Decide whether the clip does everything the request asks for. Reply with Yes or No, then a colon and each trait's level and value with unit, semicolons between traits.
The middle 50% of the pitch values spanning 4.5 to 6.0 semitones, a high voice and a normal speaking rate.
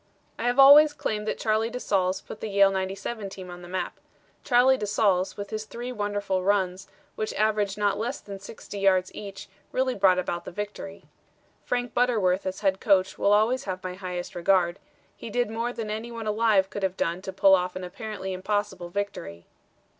No: narrow, 2.6 semitones; high, 200 Hz; average, 195 wpm